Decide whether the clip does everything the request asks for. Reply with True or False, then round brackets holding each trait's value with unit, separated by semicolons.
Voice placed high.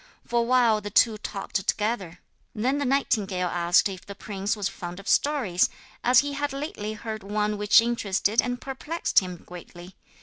True (210 Hz)